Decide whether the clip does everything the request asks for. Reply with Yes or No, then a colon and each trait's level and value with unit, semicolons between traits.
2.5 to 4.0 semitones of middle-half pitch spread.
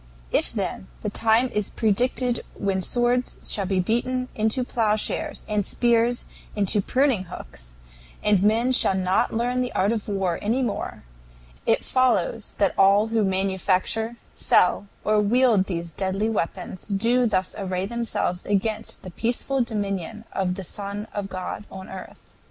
Yes: average, 3.7 semitones